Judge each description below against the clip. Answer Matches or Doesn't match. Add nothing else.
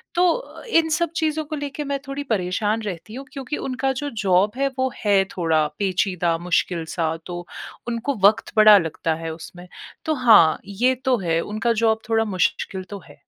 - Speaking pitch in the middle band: Doesn't match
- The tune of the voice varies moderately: Doesn't match